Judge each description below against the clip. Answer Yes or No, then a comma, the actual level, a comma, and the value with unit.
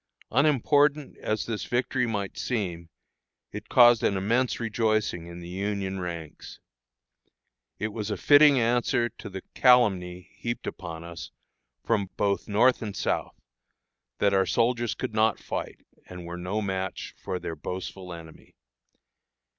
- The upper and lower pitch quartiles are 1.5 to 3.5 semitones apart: No, average, 4.6 semitones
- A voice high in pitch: No, low, 105 Hz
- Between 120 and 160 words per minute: Yes, average, 140 wpm